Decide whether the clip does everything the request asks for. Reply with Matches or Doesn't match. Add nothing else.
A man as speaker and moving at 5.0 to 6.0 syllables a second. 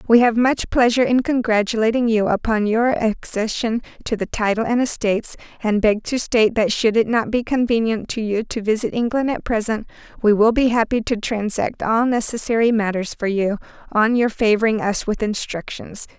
Doesn't match